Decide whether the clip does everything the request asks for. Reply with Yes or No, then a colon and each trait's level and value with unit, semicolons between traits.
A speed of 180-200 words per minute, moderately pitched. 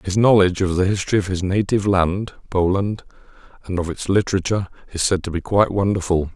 No: average, 190 wpm; very low, 95 Hz